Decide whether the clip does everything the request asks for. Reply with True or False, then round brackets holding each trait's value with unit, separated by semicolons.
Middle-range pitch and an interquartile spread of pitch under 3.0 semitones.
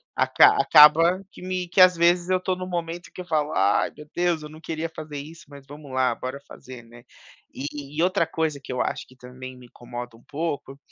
False (150 Hz; 4.9 semitones)